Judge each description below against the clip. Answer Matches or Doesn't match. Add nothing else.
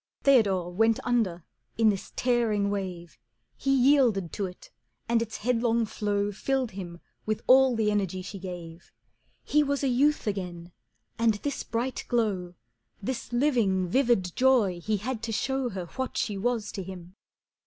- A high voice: Matches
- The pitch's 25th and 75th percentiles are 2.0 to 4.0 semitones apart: Doesn't match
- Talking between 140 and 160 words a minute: Matches